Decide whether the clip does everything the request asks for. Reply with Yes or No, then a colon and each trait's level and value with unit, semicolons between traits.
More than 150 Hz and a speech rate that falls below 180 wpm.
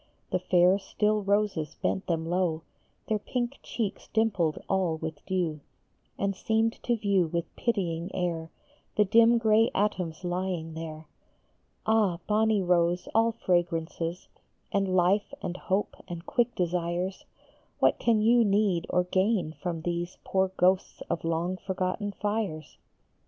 Yes: medium, 185 Hz; slow, 135 wpm